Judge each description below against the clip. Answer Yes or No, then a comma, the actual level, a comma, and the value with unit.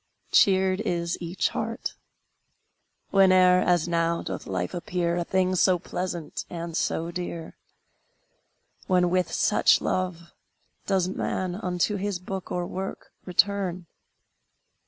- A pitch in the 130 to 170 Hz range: No, medium, 180 Hz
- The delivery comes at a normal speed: No, slow, 115 wpm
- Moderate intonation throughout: No, narrow, 1.6 semitones